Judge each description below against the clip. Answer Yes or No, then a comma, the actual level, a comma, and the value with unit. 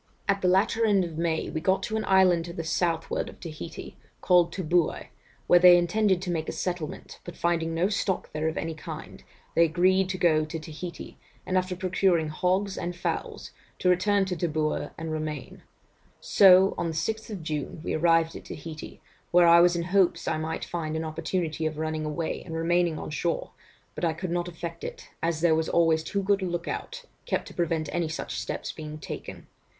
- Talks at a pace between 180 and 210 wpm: Yes, average, 200 wpm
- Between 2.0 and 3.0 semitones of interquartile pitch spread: Yes, narrow, 2.4 semitones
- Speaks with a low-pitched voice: No, medium, 170 Hz